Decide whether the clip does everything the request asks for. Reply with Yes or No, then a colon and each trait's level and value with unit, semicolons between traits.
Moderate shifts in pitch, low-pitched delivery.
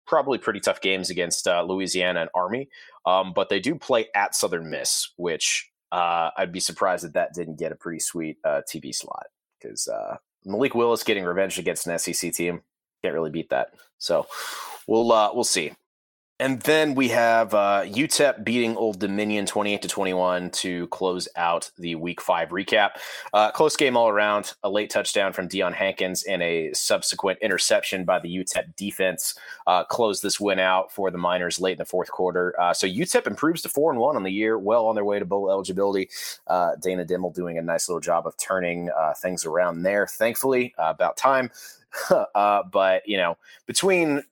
Yes: average, 3.2 semitones; very low, 95 Hz